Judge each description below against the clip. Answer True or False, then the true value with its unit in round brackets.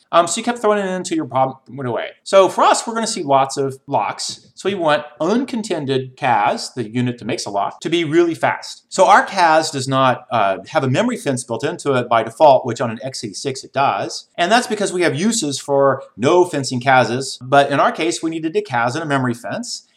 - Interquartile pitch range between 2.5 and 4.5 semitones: False (5.5 semitones)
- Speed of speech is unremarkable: False (235 wpm)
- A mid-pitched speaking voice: True (145 Hz)